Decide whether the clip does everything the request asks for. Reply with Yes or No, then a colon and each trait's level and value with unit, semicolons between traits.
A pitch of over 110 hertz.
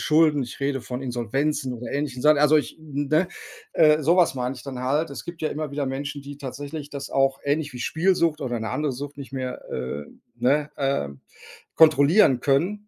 Yes: medium, 140 Hz